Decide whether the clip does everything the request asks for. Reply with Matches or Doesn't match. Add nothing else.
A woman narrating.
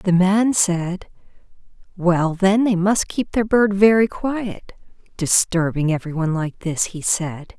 Matches